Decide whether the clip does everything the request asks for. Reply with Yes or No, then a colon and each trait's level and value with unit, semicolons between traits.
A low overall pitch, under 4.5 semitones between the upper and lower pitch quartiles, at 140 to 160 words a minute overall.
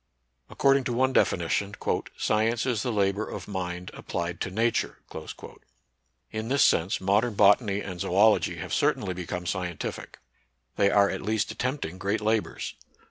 Yes: low, 100 Hz; average, 3.4 semitones; average, 150 wpm